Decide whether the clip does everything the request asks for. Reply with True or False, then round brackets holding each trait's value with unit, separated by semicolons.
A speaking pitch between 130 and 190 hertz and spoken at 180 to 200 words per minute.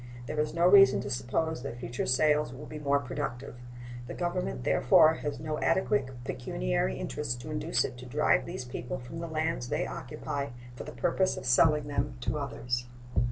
True (140 Hz; 185 wpm)